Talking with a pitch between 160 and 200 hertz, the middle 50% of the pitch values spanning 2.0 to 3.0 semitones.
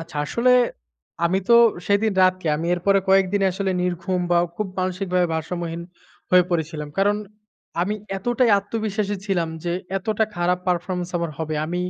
Yes: medium, 185 Hz; average, 2.7 semitones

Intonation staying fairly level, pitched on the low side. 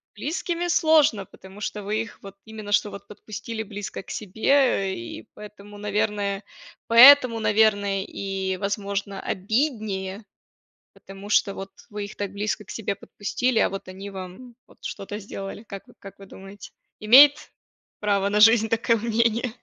No: narrow, 2.3 semitones; high, 205 Hz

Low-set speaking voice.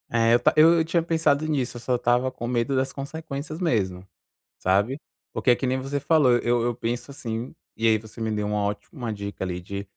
Yes: low, 120 Hz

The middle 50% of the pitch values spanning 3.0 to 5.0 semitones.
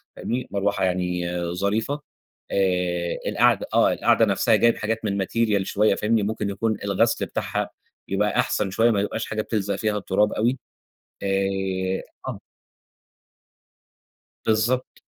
No: narrow, 2.4 semitones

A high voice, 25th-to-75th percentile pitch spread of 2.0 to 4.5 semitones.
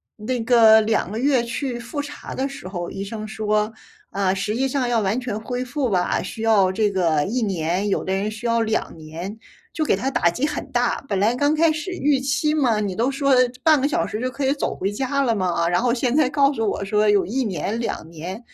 No: high, 225 Hz; average, 4.9 semitones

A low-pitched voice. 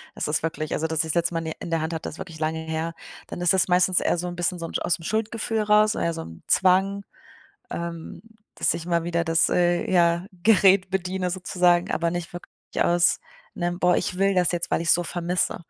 No: medium, 175 Hz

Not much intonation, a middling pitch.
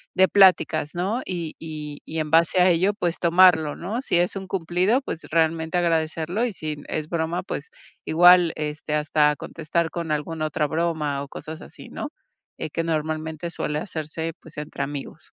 Yes: narrow, 2.3 semitones; medium, 160 Hz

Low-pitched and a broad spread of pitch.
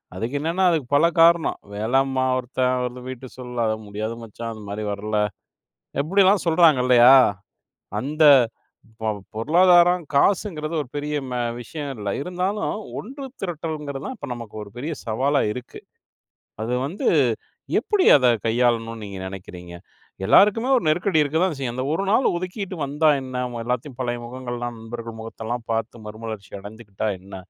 Yes: low, 130 Hz; wide, 6.0 semitones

